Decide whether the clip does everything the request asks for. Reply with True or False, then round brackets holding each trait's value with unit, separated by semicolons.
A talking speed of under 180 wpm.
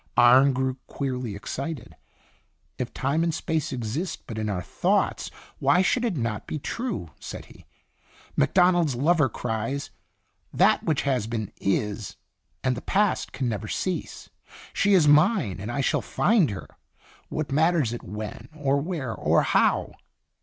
True (160 wpm)